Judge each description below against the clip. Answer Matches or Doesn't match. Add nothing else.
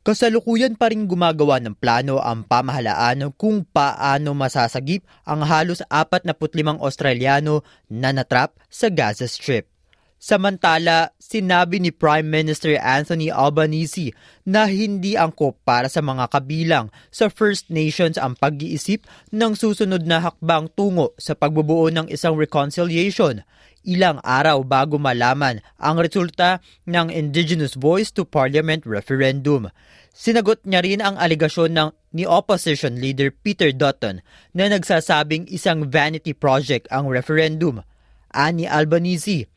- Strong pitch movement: Doesn't match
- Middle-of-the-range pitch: Matches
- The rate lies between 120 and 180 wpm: Matches